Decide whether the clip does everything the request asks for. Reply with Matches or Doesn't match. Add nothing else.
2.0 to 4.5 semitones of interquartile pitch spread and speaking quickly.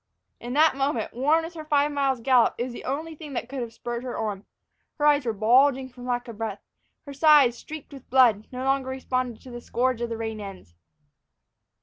Matches